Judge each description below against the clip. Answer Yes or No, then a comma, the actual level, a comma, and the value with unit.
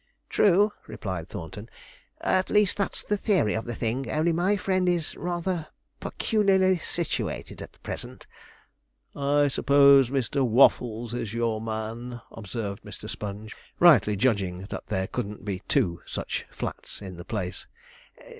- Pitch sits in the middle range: No, low, 120 Hz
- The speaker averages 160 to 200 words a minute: No, slow, 135 wpm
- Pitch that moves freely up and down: Yes, wide, 8.5 semitones